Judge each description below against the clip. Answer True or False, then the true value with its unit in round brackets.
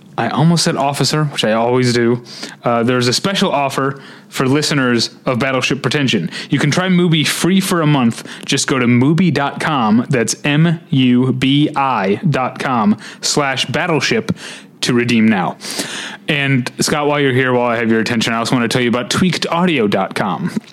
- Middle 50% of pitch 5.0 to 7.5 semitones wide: True (5.4 semitones)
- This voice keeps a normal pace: True (155 wpm)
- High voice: False (140 Hz)